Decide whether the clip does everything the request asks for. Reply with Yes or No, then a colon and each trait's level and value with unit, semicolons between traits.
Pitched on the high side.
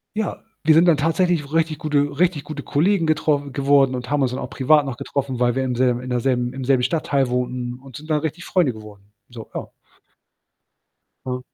No: medium, 140 Hz